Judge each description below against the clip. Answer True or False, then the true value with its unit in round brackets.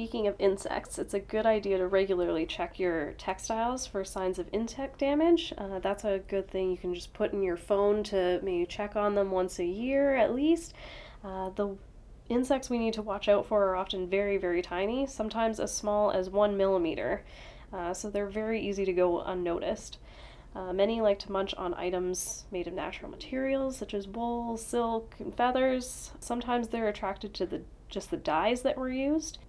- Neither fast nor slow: True (195 wpm)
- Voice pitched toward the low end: False (205 Hz)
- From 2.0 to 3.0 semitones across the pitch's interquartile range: False (3.8 semitones)